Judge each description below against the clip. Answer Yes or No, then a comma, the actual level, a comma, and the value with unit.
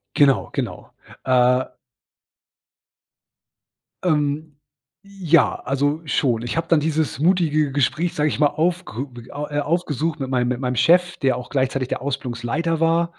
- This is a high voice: No, medium, 145 Hz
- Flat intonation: No, average, 4.0 semitones